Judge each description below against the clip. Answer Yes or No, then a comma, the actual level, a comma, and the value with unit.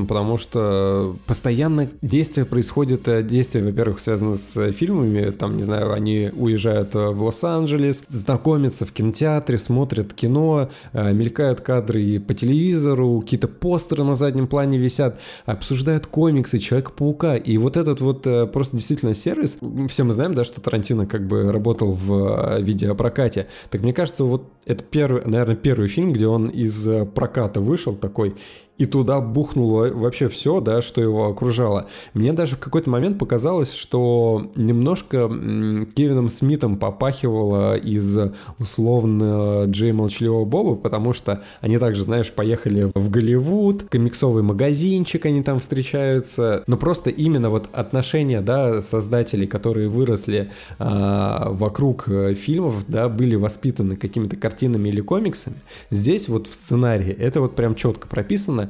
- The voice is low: Yes, low, 120 Hz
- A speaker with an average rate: Yes, average, 140 wpm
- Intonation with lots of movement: No, average, 4.2 semitones